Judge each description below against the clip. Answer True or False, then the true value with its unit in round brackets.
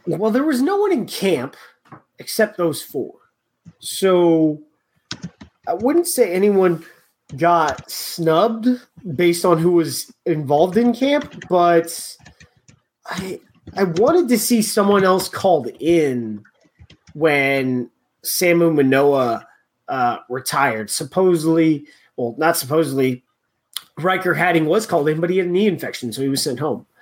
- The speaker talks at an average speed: False (130 wpm)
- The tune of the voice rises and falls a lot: False (5.0 semitones)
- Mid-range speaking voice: True (170 Hz)